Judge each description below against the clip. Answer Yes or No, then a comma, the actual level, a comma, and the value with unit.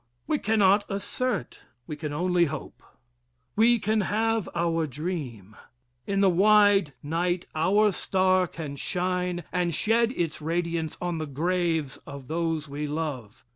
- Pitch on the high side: No, medium, 175 Hz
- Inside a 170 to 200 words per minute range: No, slow, 135 wpm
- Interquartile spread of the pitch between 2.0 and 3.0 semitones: No, average, 4.2 semitones